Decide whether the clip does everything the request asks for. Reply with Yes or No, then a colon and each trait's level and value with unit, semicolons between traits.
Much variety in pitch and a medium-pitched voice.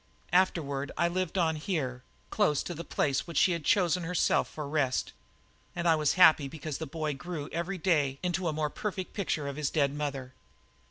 No: average, 3.5 semitones; medium, 155 Hz